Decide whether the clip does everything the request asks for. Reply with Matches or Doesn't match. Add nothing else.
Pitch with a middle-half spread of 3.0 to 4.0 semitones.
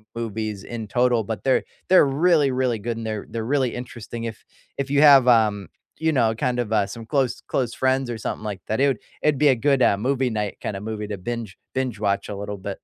Matches